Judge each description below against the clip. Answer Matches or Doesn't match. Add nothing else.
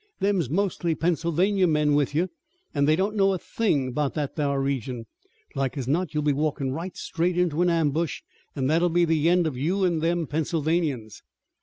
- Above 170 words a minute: Matches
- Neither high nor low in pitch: Matches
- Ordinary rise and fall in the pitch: Matches